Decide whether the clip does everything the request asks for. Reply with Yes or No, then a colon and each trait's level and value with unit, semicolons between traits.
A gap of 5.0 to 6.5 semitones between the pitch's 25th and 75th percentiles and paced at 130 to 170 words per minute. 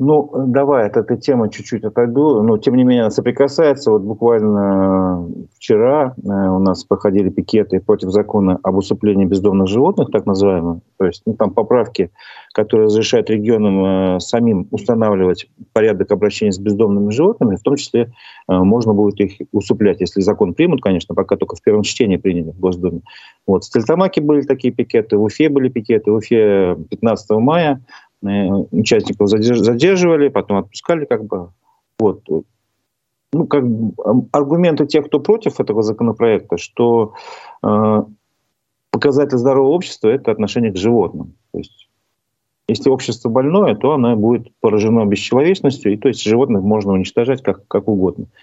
No: average, 3.8 semitones; average, 150 wpm